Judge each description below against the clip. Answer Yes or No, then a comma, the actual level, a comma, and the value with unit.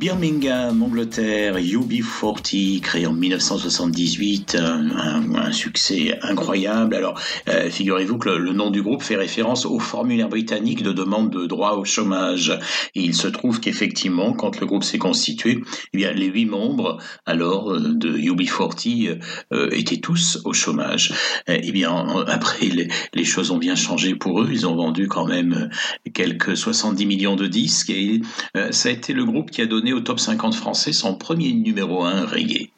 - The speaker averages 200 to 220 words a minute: No, average, 160 wpm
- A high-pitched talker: No, medium, 170 Hz